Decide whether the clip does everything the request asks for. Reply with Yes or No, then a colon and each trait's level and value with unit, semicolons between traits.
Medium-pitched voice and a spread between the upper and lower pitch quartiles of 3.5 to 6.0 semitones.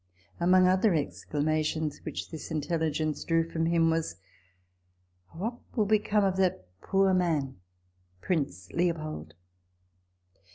Yes: medium, 160 Hz; average, 4.2 semitones